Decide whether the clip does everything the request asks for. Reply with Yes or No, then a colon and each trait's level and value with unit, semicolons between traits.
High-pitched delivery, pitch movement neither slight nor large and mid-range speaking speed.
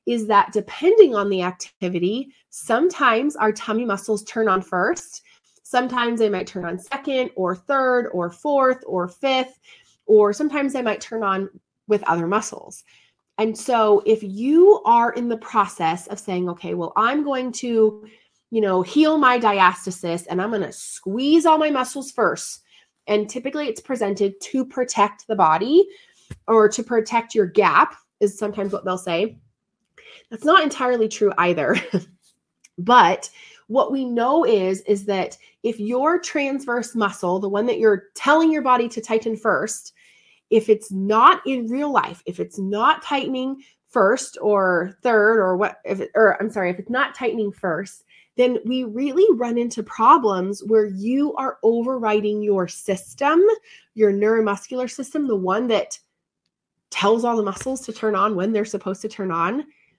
Yes: high, 220 Hz; average, 4.4 semitones; average, 165 wpm